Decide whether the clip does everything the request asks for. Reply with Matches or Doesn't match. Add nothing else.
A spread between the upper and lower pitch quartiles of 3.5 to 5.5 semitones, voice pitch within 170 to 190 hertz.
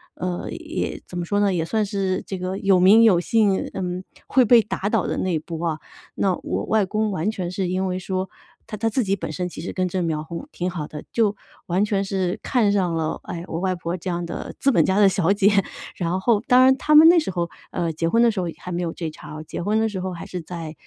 Doesn't match